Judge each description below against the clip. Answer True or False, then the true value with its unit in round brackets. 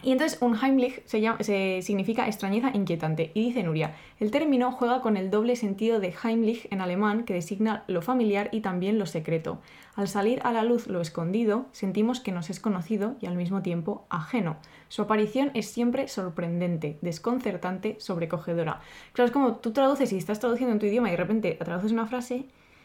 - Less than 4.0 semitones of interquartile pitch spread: False (4.7 semitones)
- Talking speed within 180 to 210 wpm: True (190 wpm)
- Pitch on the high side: True (215 Hz)